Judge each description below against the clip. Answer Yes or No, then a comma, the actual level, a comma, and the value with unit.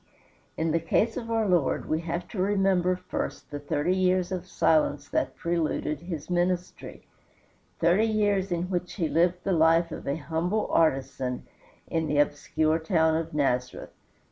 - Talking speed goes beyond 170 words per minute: No, average, 160 wpm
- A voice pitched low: No, medium, 170 Hz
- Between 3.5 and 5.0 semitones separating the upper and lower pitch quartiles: No, average, 2.7 semitones